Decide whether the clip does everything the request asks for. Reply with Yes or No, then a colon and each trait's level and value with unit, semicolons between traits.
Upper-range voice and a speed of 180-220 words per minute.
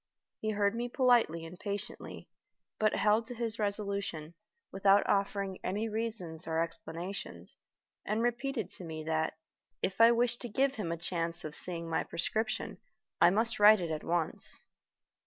No: high, 200 Hz; average, 155 wpm